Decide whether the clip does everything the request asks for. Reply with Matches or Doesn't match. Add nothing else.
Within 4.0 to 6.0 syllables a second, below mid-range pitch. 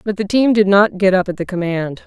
Doesn't match